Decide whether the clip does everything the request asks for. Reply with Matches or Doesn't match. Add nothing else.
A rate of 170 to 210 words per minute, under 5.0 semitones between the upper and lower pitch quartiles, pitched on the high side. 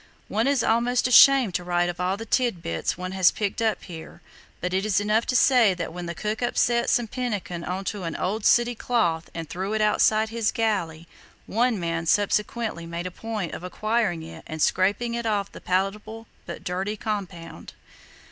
Matches